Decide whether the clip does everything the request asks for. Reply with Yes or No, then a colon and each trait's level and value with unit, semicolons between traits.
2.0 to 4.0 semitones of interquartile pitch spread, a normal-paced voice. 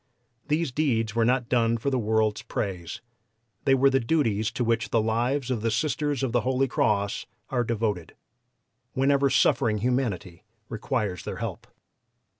Yes: average, 3.5 semitones; average, 155 wpm